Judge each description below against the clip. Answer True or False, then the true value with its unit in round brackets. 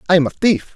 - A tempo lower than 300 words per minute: False (315 wpm)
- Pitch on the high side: False (180 Hz)